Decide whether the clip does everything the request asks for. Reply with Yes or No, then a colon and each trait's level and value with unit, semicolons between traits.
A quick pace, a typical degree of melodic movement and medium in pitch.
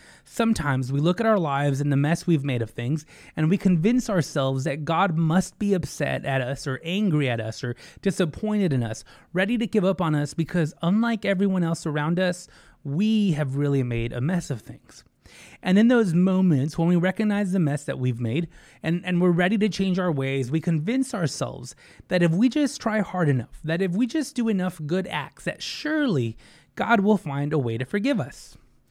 No: fast, 210 wpm; wide, 5.8 semitones; medium, 170 Hz